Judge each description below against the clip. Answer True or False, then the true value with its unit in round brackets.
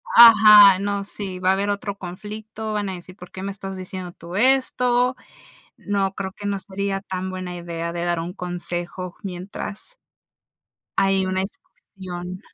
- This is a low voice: False (190 Hz)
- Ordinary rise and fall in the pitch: False (2.0 semitones)